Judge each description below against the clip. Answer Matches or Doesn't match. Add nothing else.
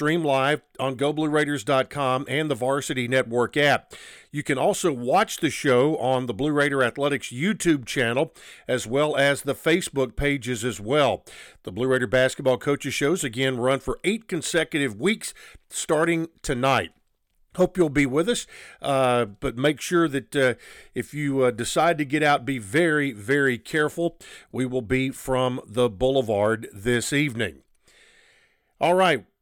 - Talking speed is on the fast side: Doesn't match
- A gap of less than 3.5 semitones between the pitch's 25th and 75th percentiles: Matches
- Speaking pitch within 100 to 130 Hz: Doesn't match